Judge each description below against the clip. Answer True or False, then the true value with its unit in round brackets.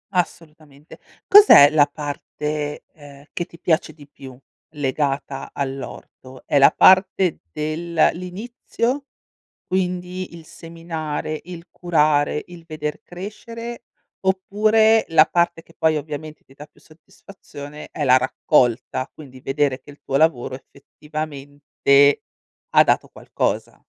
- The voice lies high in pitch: False (155 Hz)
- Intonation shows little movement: False (3.7 semitones)